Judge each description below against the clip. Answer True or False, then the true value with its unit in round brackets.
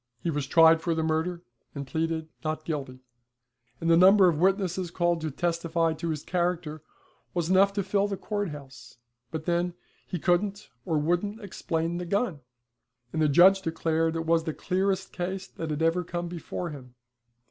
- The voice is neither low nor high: True (170 Hz)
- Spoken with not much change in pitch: True (2.3 semitones)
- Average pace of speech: True (180 wpm)